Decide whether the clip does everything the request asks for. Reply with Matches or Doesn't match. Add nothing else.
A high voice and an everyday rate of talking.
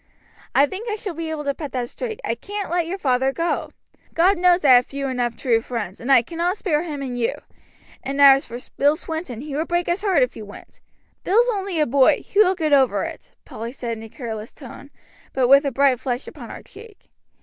Doesn't match